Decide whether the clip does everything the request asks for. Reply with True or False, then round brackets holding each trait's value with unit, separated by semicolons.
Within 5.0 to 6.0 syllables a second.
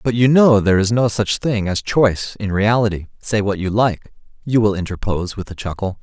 True (5.5 syllables/s)